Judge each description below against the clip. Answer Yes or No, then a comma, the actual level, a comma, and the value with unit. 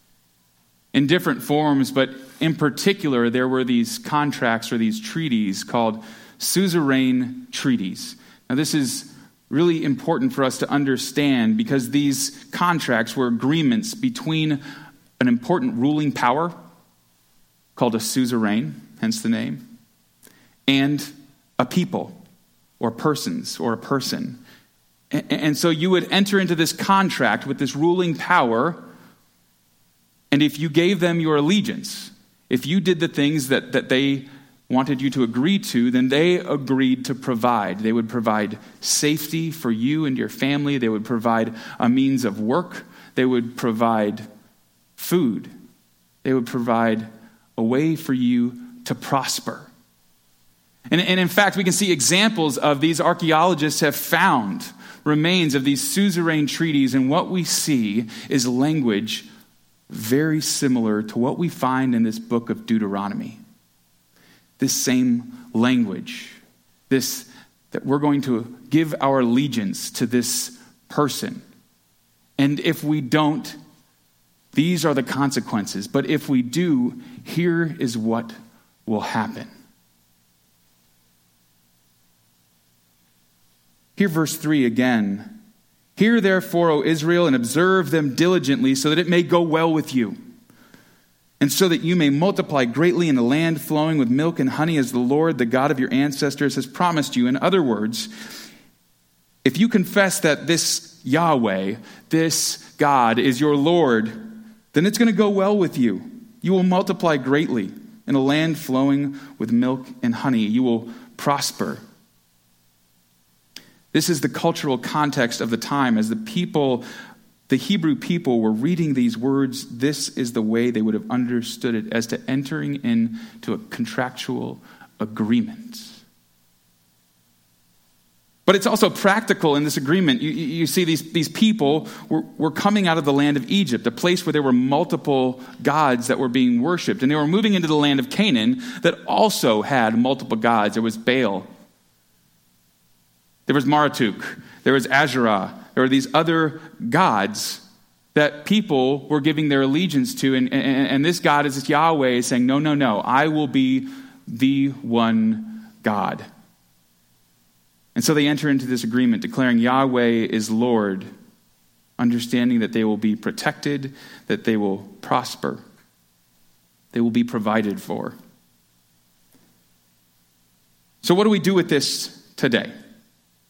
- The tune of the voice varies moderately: No, wide, 7.2 semitones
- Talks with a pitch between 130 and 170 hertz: Yes, medium, 140 Hz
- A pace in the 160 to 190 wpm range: No, average, 145 wpm